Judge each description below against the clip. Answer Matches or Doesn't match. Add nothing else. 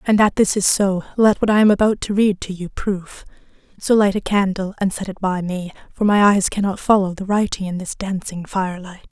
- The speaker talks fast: Matches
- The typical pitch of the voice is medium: Doesn't match